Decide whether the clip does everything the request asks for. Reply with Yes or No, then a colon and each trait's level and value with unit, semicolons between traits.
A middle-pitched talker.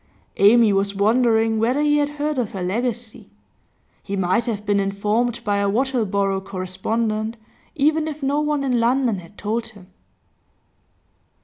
No: high, 225 Hz